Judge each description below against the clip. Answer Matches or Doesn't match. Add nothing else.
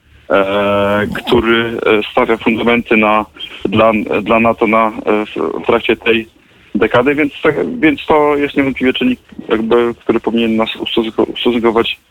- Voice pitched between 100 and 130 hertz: Matches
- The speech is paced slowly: Doesn't match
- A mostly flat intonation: Matches